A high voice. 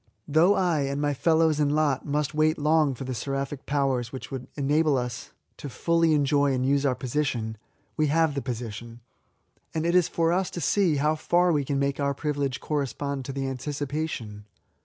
No: medium, 145 Hz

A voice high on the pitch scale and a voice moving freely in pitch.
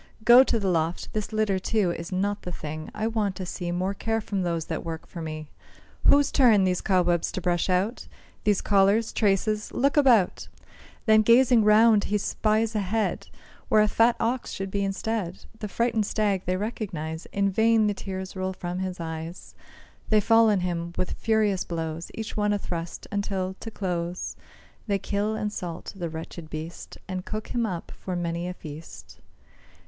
No: high, 195 Hz; average, 3.6 semitones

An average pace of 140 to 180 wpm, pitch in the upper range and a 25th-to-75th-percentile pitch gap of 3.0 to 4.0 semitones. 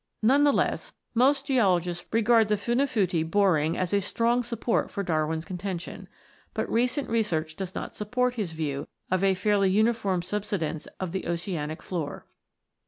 No: average, 155 wpm; high, 195 Hz; average, 5.1 semitones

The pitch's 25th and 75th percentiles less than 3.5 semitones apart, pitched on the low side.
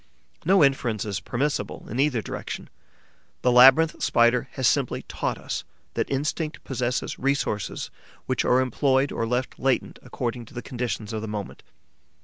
Yes: narrow, 2.6 semitones; low, 125 Hz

